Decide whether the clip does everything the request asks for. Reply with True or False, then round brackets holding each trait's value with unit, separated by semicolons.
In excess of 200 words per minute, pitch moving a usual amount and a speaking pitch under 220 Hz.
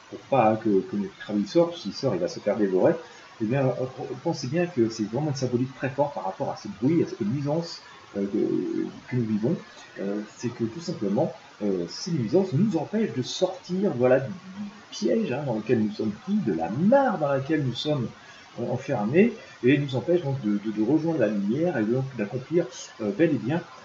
False (220 wpm; 7.4 semitones; 140 Hz)